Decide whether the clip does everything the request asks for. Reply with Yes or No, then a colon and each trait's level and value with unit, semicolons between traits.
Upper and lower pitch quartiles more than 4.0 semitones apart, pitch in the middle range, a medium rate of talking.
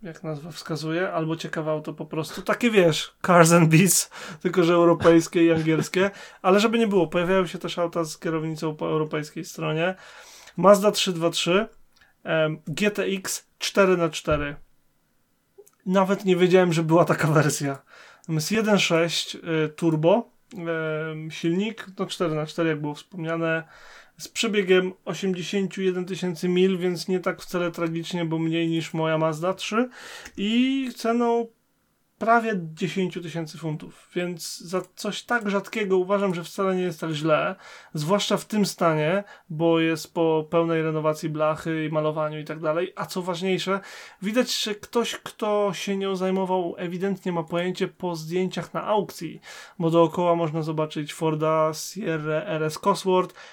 No: average, 3.2 semitones; medium, 175 Hz; average, 140 wpm